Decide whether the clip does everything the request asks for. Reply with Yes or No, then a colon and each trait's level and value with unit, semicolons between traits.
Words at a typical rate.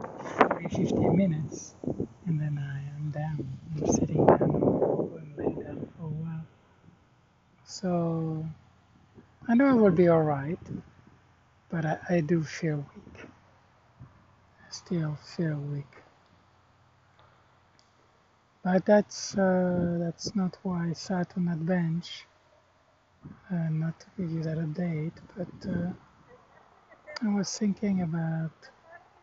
No: slow, 115 wpm